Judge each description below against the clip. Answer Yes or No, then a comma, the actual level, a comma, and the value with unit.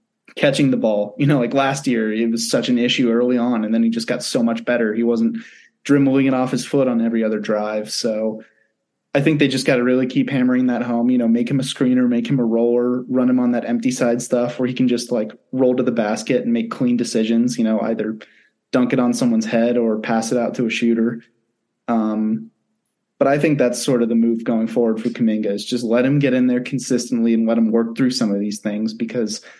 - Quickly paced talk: Yes, fast, 245 wpm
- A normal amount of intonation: No, narrow, 1.8 semitones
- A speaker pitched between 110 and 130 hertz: Yes, low, 120 Hz